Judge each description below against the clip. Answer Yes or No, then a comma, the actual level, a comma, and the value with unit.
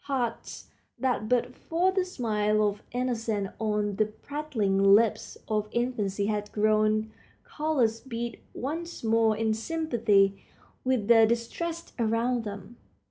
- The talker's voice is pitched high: Yes, high, 225 Hz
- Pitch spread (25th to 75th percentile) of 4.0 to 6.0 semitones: No, average, 3.1 semitones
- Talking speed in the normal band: No, slow, 125 wpm